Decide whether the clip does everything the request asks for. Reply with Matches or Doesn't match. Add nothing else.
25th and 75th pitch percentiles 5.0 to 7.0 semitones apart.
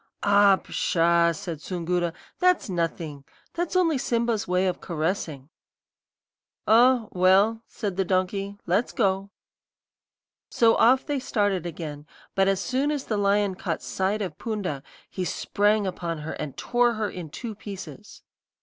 Doesn't match